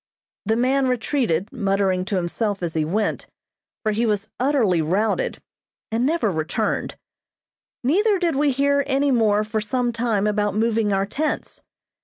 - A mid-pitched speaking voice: No, high, 220 Hz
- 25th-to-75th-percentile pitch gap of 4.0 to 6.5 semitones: Yes, average, 4.9 semitones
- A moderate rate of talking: Yes, average, 150 wpm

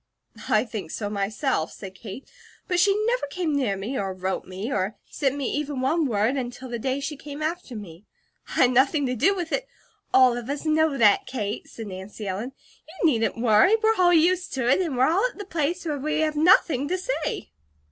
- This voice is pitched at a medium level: No, very high, 270 Hz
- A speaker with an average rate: No, fast, 220 wpm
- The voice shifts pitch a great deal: Yes, wide, 6.7 semitones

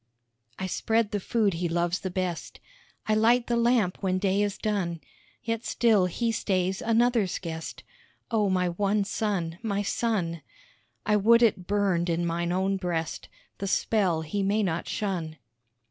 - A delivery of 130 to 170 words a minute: Yes, average, 160 wpm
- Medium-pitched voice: No, high, 195 Hz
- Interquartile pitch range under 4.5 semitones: Yes, average, 3.7 semitones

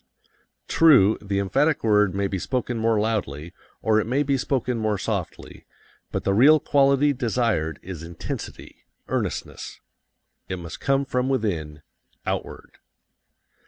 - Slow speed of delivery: Yes, slow, 130 wpm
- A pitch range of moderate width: No, wide, 5.7 semitones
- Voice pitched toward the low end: Yes, low, 110 Hz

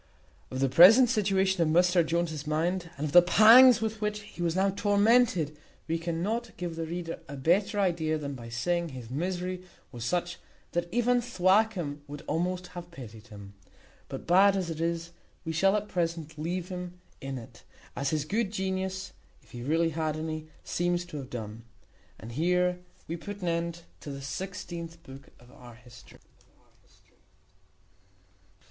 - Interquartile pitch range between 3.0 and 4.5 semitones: Yes, average, 3.7 semitones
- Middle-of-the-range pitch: Yes, medium, 170 Hz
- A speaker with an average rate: Yes, average, 165 wpm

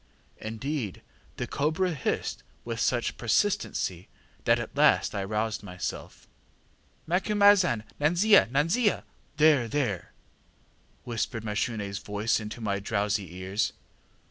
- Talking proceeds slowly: Yes, slow, 105 wpm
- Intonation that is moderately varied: No, wide, 6.8 semitones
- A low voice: Yes, low, 115 Hz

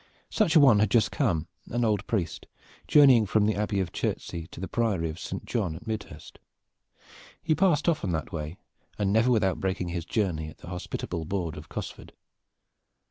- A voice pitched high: No, low, 100 Hz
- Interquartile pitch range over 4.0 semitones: Yes, average, 5.2 semitones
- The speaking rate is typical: Yes, average, 185 wpm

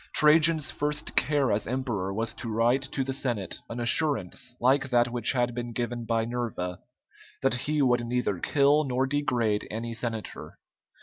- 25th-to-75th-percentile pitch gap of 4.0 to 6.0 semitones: No, average, 2.9 semitones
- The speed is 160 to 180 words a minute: Yes, average, 165 wpm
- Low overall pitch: Yes, low, 120 Hz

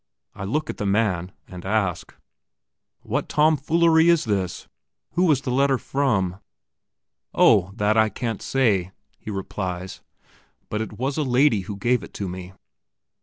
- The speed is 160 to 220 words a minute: No, average, 150 wpm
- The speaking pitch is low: Yes, low, 110 Hz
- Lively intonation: Yes, wide, 6.3 semitones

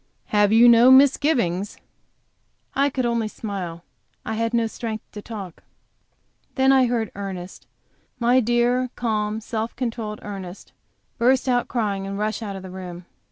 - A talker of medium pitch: No, high, 220 Hz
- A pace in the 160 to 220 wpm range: No, average, 150 wpm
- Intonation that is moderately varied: Yes, average, 3.4 semitones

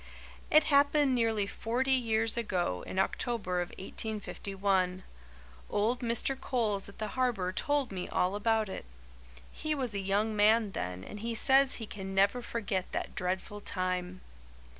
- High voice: Yes, high, 210 Hz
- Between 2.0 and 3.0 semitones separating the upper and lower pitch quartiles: No, average, 4.0 semitones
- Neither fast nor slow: Yes, average, 150 wpm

